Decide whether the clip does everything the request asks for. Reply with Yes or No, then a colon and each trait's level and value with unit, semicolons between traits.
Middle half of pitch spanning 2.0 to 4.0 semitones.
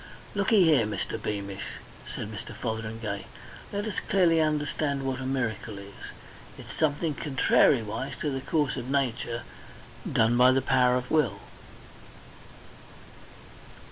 No: average, 5.0 semitones